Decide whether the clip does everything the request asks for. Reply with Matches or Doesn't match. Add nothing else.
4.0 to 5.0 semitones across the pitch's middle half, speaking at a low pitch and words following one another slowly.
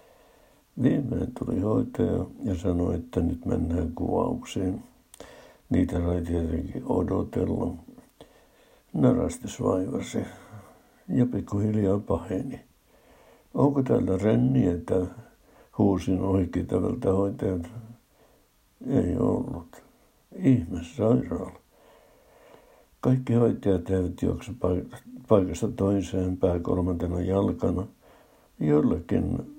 Matches